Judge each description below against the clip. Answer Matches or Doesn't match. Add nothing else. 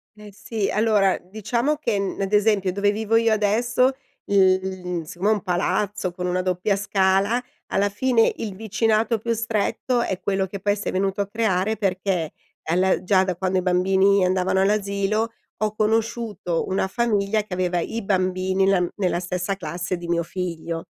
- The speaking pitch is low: Doesn't match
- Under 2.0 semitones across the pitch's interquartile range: Doesn't match